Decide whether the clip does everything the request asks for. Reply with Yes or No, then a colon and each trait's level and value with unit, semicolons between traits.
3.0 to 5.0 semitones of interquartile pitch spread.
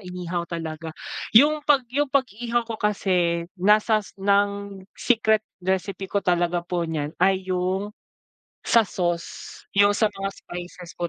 Yes: average, 3.3 semitones